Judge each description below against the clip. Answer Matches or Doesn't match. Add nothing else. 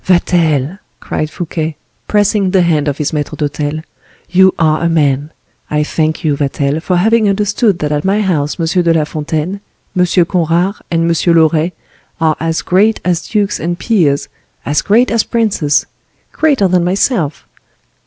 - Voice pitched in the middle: Matches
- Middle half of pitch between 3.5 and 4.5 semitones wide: Matches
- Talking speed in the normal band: Matches